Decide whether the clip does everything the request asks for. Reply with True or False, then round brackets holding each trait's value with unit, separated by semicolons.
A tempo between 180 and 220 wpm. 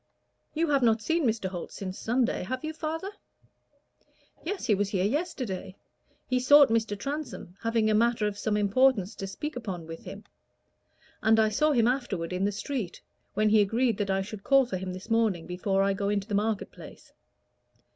True (190 wpm)